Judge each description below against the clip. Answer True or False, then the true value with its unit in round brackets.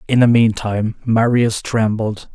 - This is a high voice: False (110 Hz)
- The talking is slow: True (130 wpm)